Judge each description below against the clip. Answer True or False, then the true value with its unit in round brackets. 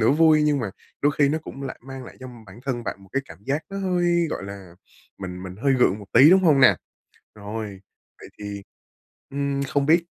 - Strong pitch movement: True (6.7 semitones)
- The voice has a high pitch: False (135 Hz)